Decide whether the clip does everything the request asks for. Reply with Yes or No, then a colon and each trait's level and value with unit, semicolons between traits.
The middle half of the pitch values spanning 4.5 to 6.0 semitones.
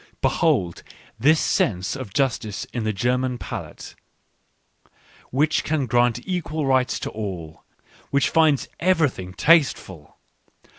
Yes: wide, 5.6 semitones